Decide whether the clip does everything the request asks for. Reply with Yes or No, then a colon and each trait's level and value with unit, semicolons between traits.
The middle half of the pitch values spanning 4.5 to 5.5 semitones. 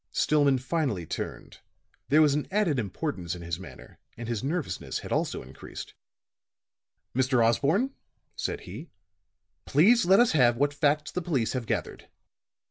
Yes: average, 5.2 semitones